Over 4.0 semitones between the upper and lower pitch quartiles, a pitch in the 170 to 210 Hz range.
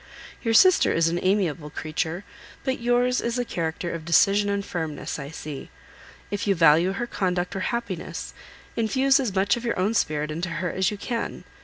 Yes: wide, 5.6 semitones; high, 190 Hz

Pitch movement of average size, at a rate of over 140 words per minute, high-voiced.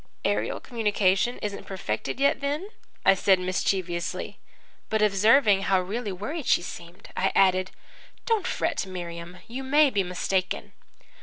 No: average, 4.6 semitones; slow, 135 wpm; high, 195 Hz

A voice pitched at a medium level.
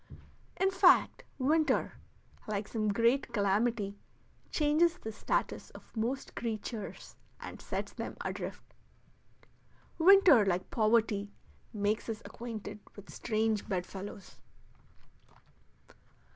No: high, 220 Hz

